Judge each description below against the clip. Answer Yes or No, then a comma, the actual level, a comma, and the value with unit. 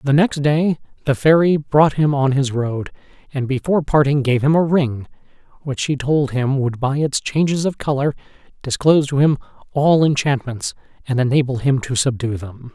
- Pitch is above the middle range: No, medium, 140 Hz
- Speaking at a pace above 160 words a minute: Yes, average, 180 wpm